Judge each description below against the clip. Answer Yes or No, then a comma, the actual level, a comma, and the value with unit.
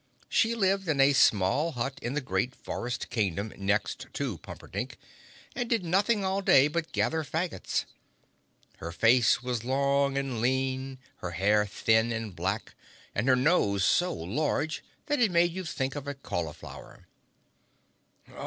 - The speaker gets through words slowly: No, average, 150 wpm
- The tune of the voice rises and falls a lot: Yes, wide, 6.6 semitones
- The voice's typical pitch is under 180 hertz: Yes, low, 135 Hz